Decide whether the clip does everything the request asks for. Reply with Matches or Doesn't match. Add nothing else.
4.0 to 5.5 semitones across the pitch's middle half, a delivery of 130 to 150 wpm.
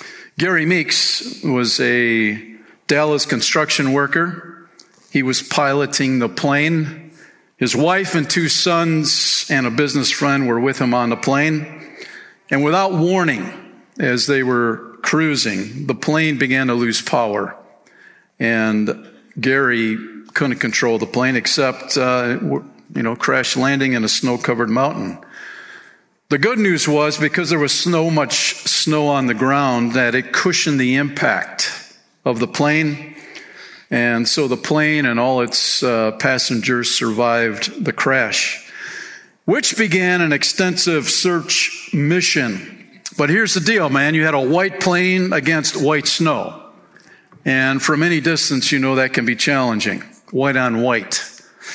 Matches